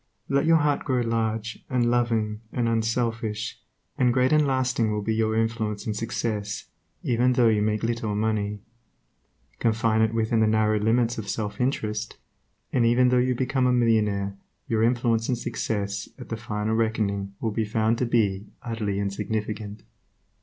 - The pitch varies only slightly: Yes, narrow, 2.1 semitones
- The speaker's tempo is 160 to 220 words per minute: Yes, average, 165 wpm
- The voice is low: Yes, low, 110 Hz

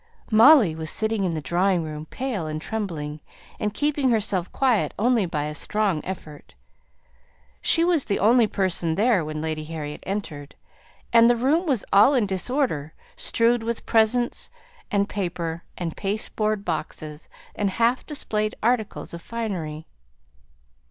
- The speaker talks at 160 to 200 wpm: No, average, 140 wpm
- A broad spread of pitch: Yes, wide, 6.3 semitones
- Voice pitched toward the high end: Yes, high, 200 Hz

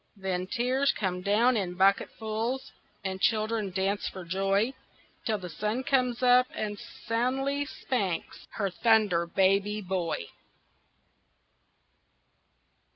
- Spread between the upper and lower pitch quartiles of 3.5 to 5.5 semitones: Yes, average, 4.0 semitones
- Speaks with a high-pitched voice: Yes, high, 210 Hz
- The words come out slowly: Yes, slow, 105 wpm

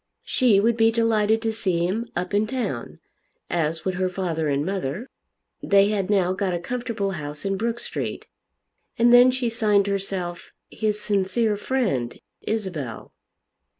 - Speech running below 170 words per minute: Yes, average, 150 wpm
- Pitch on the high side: Yes, high, 200 Hz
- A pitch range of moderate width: Yes, average, 4.1 semitones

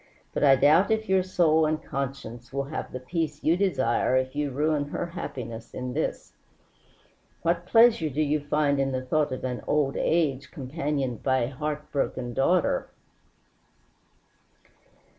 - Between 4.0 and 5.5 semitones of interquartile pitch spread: No, average, 3.4 semitones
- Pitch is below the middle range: No, medium, 145 Hz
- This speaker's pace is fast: No, average, 155 wpm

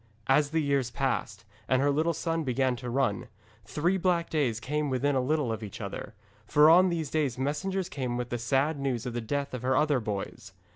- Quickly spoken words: Yes, fast, 210 wpm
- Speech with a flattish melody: No, average, 3.8 semitones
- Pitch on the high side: No, medium, 140 Hz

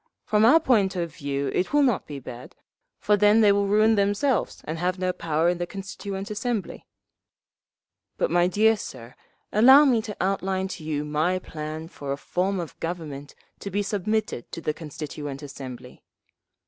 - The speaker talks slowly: No, average, 175 wpm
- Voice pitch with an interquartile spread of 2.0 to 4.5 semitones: No, average, 5.2 semitones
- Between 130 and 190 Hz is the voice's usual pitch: Yes, medium, 185 Hz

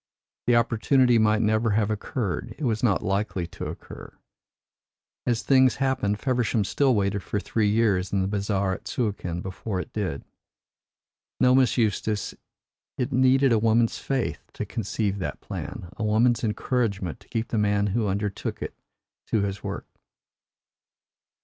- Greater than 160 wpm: No, average, 150 wpm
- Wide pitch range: No, average, 3.2 semitones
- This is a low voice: Yes, low, 110 Hz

